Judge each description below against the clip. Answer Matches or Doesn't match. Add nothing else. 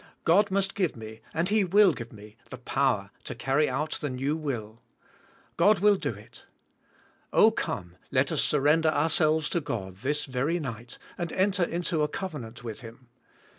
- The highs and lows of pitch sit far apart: Matches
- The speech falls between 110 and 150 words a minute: Doesn't match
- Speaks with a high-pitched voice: Doesn't match